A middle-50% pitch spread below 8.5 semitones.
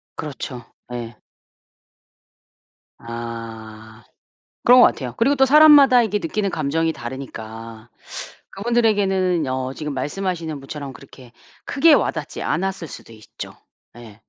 No: wide, 8.9 semitones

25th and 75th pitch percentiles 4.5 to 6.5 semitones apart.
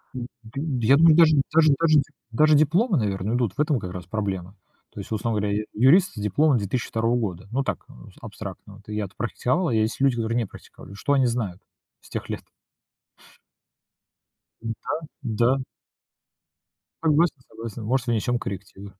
Yes: average, 5.1 semitones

